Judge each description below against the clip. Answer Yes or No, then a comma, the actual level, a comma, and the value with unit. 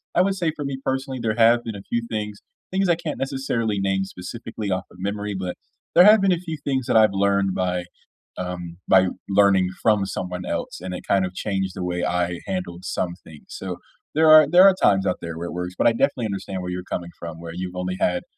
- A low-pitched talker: Yes, low, 100 Hz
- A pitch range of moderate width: Yes, average, 4.8 semitones